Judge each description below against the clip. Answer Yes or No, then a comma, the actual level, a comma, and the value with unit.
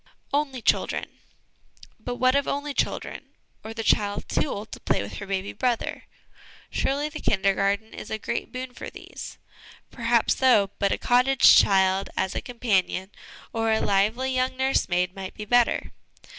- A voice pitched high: Yes, high, 225 Hz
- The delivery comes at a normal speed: Yes, average, 165 wpm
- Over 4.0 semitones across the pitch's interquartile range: Yes, average, 4.4 semitones